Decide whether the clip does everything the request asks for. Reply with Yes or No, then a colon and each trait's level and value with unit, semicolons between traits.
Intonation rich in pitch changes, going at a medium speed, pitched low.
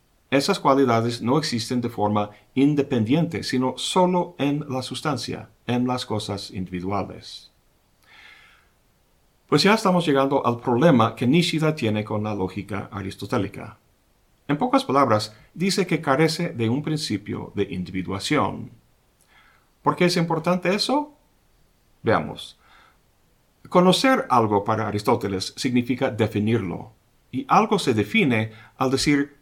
No: wide, 5.7 semitones; slow, 120 wpm; low, 125 Hz